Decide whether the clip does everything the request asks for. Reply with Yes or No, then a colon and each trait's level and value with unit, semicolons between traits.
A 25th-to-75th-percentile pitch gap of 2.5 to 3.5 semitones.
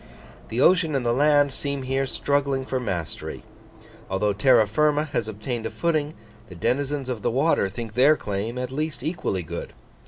No: average, 4.6 semitones